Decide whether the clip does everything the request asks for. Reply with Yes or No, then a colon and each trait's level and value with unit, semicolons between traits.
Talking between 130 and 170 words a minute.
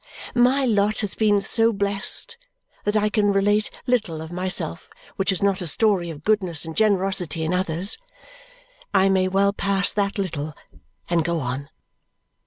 Yes: average, 160 wpm